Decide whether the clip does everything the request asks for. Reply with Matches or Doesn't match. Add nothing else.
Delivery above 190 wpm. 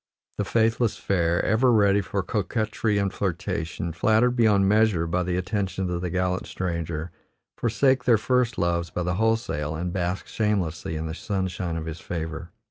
Doesn't match